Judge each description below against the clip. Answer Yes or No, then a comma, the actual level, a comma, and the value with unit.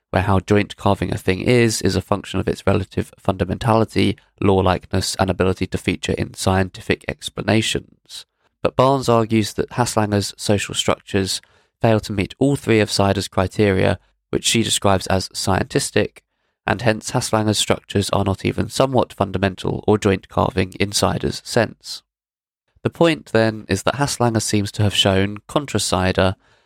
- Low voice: Yes, low, 100 Hz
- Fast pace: No, average, 155 wpm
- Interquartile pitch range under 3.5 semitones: Yes, average, 2.7 semitones